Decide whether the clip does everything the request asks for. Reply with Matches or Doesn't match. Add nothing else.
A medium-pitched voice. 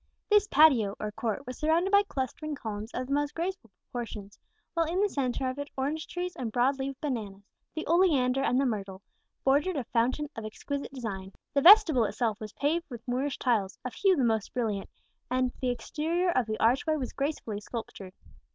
Doesn't match